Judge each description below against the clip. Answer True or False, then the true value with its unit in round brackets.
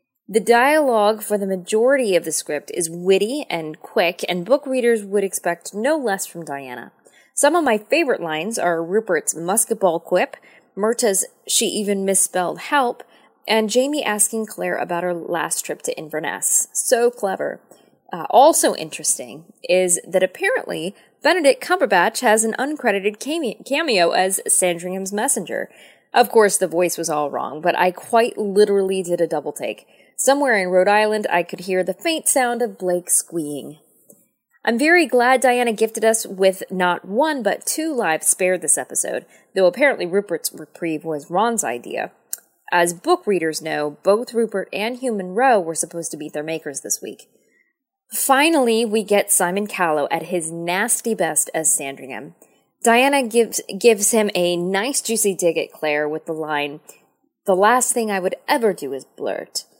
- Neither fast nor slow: True (165 wpm)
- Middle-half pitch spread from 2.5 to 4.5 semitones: False (5.6 semitones)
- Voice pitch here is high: True (200 Hz)